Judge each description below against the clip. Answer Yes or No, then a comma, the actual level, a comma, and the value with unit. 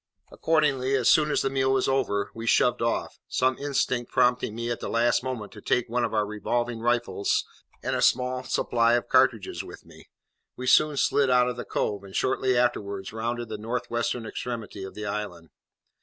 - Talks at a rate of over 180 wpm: Yes, average, 195 wpm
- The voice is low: Yes, low, 120 Hz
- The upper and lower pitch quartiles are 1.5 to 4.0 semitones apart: Yes, narrow, 2.5 semitones